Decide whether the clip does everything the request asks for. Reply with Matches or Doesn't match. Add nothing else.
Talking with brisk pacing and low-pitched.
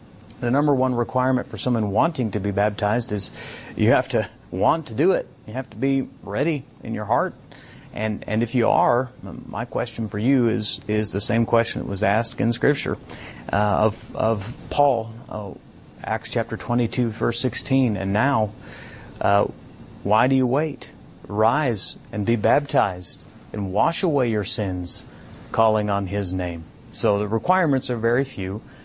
Doesn't match